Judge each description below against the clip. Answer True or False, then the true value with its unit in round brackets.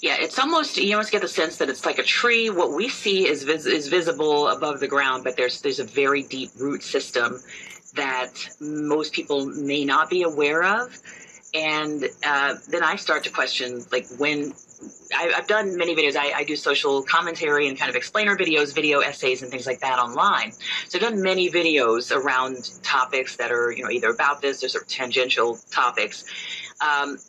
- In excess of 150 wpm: True (200 wpm)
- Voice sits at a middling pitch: True (145 Hz)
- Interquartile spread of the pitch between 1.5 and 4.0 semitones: False (4.6 semitones)